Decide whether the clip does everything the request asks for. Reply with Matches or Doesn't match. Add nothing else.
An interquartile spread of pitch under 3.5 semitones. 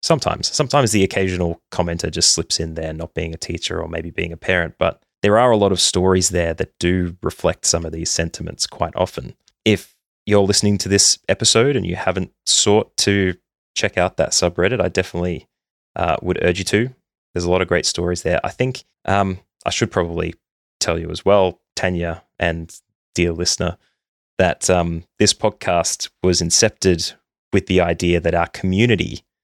Matches